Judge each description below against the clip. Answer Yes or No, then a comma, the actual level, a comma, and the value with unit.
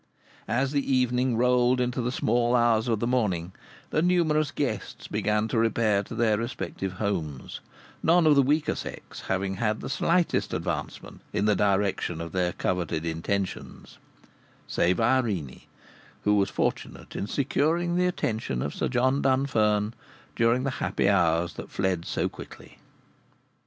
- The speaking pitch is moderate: No, low, 115 Hz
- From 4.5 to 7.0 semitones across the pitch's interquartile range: Yes, average, 5.0 semitones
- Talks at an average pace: Yes, average, 150 wpm